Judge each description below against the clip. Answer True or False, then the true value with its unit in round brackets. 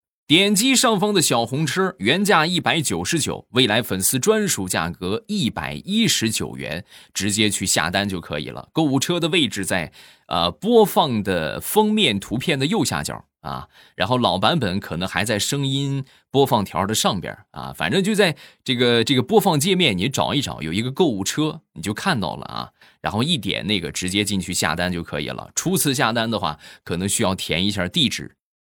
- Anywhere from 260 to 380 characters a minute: True (285 characters per minute)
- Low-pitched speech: True (125 Hz)